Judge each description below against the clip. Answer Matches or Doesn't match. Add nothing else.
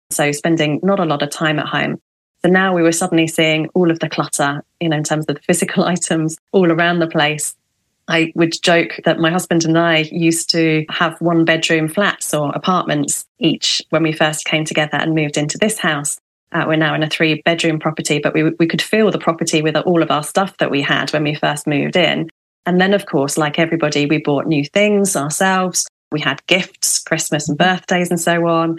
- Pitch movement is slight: Matches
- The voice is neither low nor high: Matches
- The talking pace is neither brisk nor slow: Doesn't match